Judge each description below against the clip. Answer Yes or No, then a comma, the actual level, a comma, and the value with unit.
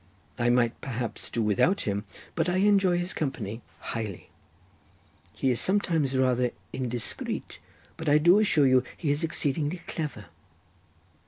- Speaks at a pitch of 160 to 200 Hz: No, low, 135 Hz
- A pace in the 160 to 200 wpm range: No, average, 140 wpm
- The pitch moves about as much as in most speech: No, wide, 5.9 semitones